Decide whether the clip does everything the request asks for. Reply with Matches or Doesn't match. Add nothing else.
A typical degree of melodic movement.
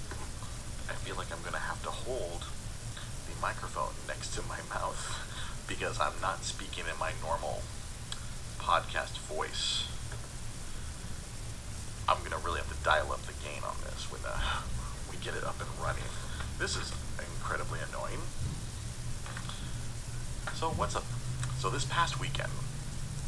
Doesn't match